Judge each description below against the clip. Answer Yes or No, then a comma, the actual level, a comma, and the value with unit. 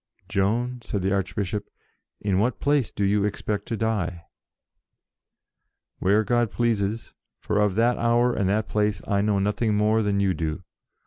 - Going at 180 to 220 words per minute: No, average, 155 wpm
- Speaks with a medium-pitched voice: No, low, 105 Hz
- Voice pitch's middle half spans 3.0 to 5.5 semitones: No, narrow, 2.4 semitones